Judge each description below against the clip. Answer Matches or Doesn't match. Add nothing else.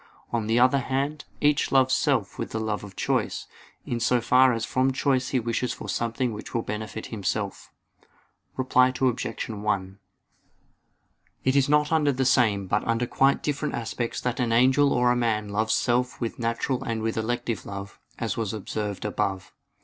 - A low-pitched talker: Matches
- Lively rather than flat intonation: Doesn't match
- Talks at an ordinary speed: Matches